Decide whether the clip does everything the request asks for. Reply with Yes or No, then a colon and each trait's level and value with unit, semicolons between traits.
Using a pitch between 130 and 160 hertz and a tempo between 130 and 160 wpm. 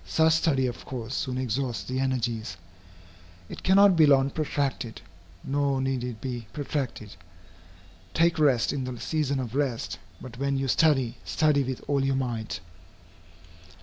Yes: low, 135 Hz; average, 150 wpm